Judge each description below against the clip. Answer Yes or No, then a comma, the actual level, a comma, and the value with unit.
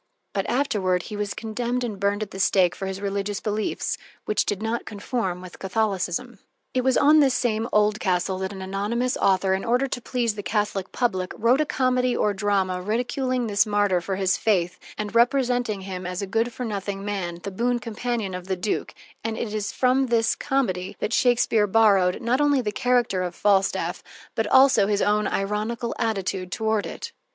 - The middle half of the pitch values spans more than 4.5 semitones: No, average, 3.8 semitones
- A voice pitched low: No, high, 210 Hz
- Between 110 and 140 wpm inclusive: No, average, 190 wpm